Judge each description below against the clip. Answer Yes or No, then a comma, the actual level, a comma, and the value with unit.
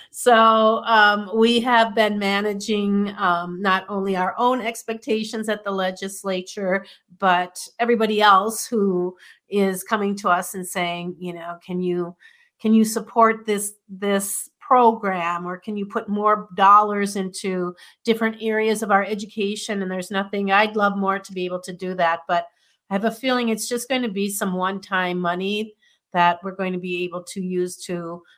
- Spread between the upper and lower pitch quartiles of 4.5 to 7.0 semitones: No, average, 3.1 semitones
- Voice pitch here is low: No, high, 200 Hz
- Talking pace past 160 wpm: Yes, average, 170 wpm